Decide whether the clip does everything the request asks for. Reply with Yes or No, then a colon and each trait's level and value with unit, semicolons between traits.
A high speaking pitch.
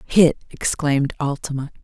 No: medium, 145 Hz